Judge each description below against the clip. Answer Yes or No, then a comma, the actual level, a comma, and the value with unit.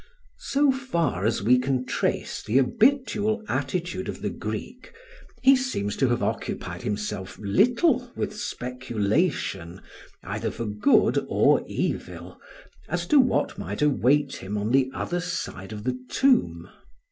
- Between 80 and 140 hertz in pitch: Yes, low, 135 Hz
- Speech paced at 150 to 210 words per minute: No, slow, 135 wpm